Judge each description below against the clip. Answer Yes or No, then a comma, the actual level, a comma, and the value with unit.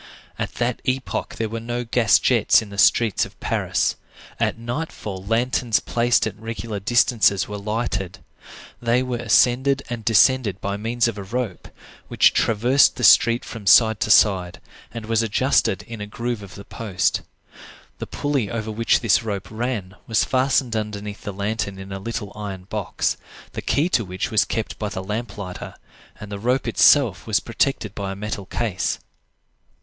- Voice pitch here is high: No, low, 110 Hz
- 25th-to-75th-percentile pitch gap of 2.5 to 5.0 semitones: Yes, average, 3.0 semitones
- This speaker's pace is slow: No, average, 175 wpm